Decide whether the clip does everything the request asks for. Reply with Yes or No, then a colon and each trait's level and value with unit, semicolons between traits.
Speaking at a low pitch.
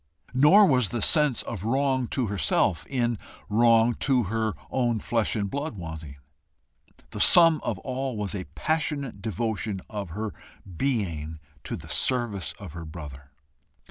Yes: low, 115 Hz